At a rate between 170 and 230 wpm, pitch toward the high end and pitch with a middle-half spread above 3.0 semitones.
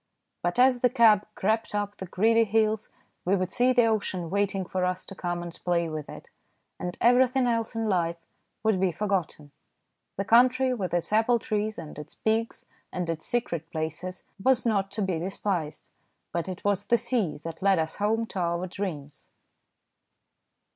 Yes: average, 175 wpm; high, 195 Hz; average, 4.3 semitones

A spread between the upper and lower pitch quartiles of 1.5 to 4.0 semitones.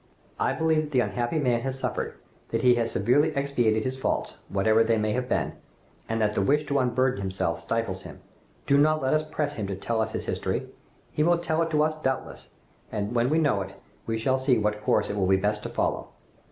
No: average, 5.3 semitones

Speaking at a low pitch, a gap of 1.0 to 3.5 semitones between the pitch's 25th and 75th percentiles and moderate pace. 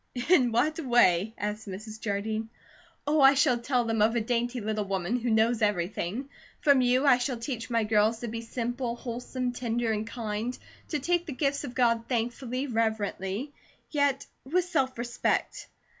No: high, 235 Hz; average, 3.0 semitones; average, 170 wpm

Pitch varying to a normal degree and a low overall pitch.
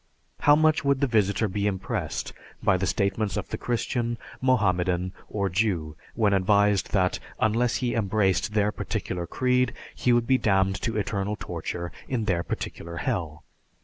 Yes: average, 4.0 semitones; low, 105 Hz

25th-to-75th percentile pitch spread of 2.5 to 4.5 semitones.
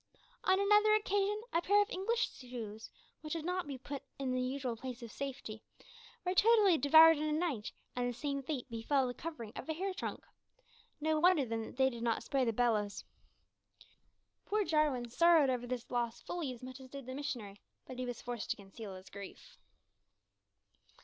No: wide, 5.6 semitones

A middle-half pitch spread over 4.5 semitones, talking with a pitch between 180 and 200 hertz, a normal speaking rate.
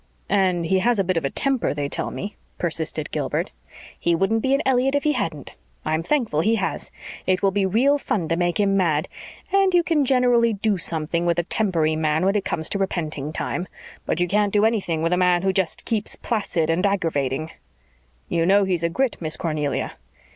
No: average, 5.0 semitones; medium, 185 Hz; fast, 210 wpm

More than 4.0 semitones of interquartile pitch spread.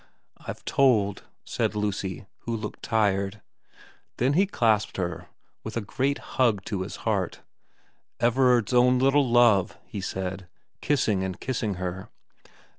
Yes: average, 4.4 semitones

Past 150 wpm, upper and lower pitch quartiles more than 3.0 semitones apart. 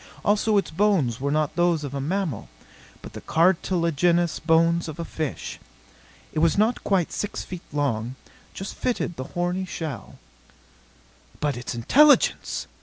No: average, 145 wpm; average, 4.4 semitones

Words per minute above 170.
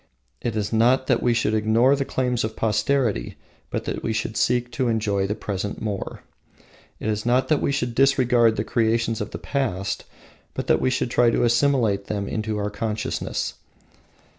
Yes: average, 185 wpm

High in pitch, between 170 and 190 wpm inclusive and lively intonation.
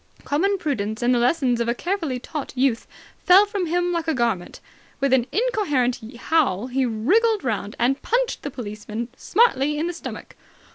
Yes: very high, 270 Hz; average, 175 wpm; wide, 6.8 semitones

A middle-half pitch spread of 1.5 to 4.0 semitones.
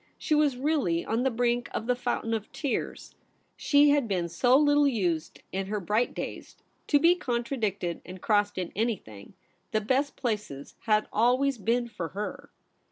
No: average, 4.8 semitones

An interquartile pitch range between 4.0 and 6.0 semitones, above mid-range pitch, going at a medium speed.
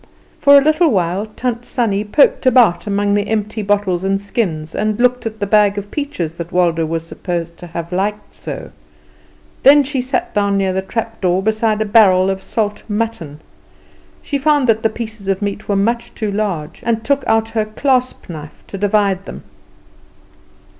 No: average, 3.2 semitones; high, 210 Hz; average, 180 wpm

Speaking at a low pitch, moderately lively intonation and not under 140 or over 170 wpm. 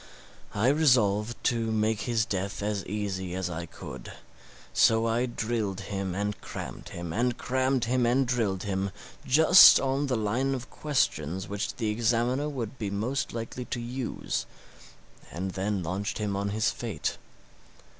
Yes: low, 110 Hz; average, 3.9 semitones; average, 155 wpm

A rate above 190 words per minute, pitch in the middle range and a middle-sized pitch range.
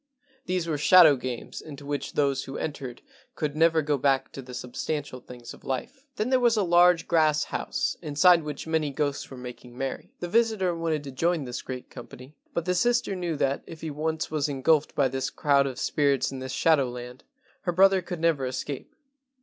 Yes: average, 200 wpm; medium, 150 Hz; average, 4.2 semitones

